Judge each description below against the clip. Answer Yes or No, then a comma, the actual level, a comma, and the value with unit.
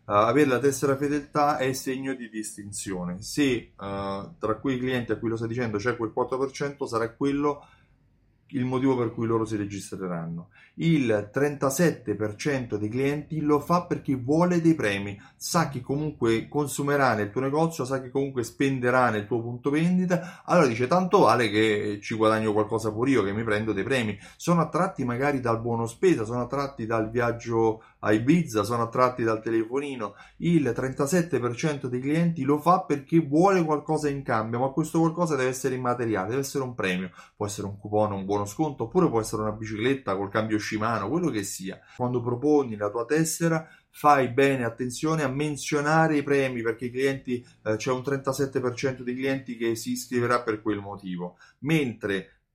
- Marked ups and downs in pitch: No, average, 4.9 semitones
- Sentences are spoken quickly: Yes, fast, 175 wpm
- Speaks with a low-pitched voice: Yes, low, 125 Hz